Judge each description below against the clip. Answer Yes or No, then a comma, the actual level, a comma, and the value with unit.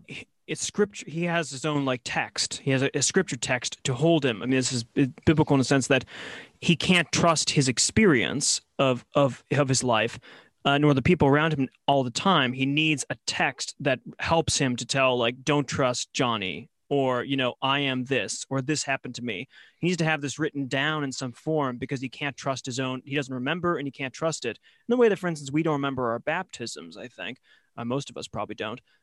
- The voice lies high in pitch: No, medium, 140 Hz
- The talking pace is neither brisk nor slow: No, fast, 230 wpm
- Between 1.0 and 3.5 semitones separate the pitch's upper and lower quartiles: Yes, average, 3.1 semitones